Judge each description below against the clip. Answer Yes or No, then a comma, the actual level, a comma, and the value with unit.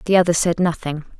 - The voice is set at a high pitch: No, medium, 170 Hz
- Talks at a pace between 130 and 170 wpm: No, average, 200 wpm